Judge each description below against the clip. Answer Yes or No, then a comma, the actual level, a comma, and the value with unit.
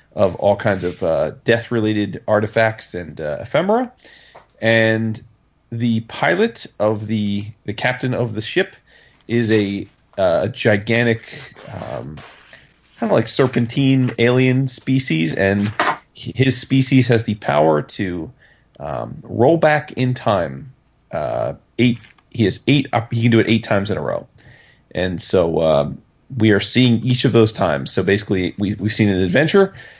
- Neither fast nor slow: Yes, average, 150 wpm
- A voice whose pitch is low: Yes, low, 115 Hz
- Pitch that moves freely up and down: No, average, 3.2 semitones